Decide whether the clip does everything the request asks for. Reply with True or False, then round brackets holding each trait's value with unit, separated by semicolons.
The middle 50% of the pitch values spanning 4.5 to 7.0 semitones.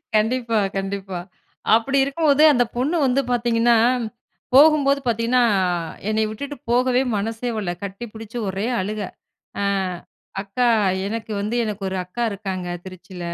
False (3.9 semitones)